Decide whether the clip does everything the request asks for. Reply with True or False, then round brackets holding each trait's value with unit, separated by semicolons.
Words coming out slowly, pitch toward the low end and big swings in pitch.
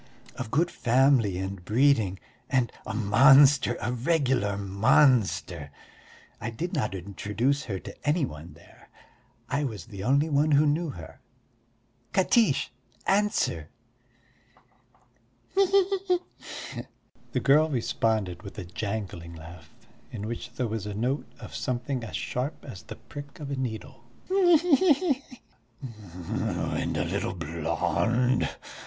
True (130 wpm; 120 Hz; 6.5 semitones)